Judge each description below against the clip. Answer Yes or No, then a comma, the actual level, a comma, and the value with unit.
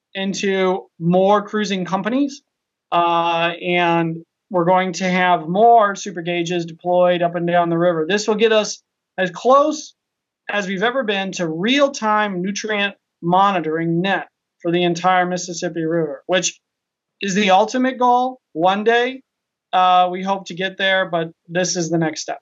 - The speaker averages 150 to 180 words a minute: Yes, average, 160 wpm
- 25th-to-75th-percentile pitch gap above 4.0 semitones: No, average, 3.1 semitones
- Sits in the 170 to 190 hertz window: Yes, medium, 185 Hz